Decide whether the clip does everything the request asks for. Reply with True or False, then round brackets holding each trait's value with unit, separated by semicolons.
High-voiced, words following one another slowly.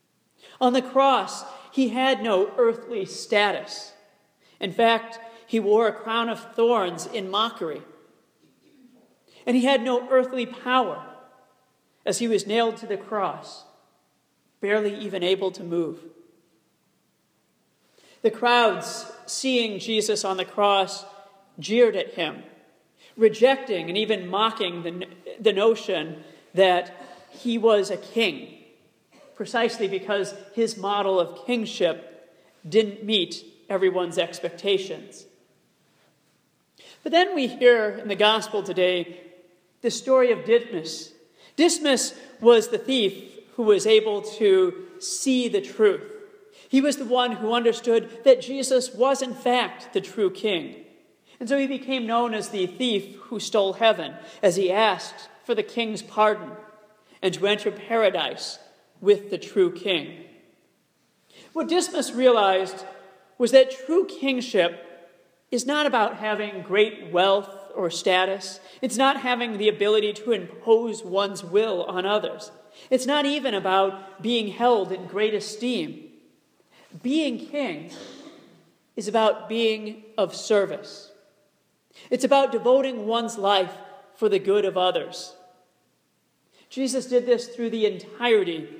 True (215 Hz; 130 wpm)